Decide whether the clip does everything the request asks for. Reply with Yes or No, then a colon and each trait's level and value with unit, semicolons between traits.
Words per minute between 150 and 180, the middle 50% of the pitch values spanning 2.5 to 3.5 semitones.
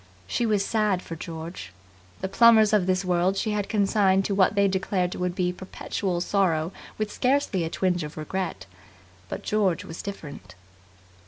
Yes: average, 165 wpm; average, 2.9 semitones